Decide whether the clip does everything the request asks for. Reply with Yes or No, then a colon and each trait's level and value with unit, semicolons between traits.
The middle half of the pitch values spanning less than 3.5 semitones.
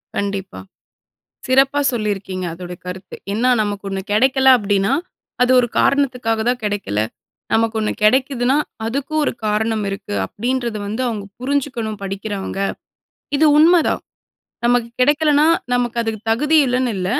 No: average, 4.2 semitones